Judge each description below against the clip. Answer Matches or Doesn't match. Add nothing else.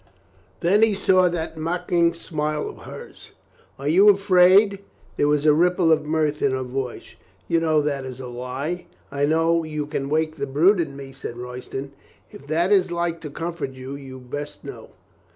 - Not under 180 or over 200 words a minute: Matches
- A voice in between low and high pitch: Matches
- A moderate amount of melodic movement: Matches